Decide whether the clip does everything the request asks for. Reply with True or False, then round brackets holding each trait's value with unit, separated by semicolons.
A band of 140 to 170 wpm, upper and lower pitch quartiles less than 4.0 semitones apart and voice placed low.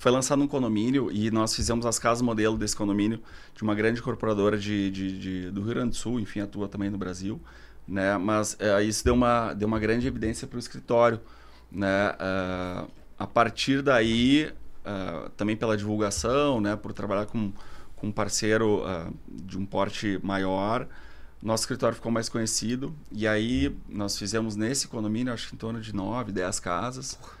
False (180 wpm; 2.9 semitones; 105 Hz)